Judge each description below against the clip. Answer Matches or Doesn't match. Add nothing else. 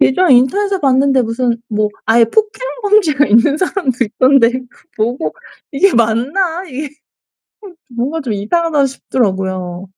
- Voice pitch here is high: Matches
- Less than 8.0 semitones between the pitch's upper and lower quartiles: Matches